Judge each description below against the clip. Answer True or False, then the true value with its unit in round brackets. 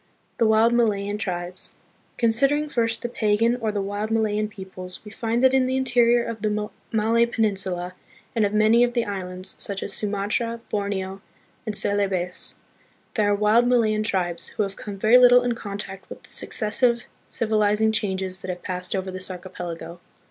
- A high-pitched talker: True (210 Hz)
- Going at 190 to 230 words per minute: False (170 wpm)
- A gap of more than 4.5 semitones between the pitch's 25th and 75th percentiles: False (3.3 semitones)